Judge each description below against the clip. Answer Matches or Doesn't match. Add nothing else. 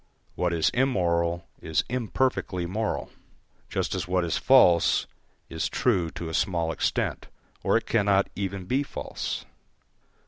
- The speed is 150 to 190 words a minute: Doesn't match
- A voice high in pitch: Doesn't match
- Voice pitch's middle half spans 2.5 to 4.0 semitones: Doesn't match